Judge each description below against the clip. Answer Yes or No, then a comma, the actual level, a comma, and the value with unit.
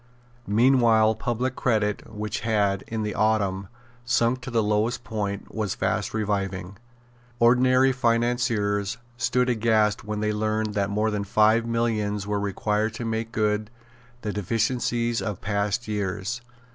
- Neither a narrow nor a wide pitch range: No, narrow, 2.1 semitones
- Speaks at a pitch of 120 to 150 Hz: No, low, 110 Hz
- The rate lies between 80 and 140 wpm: Yes, slow, 135 wpm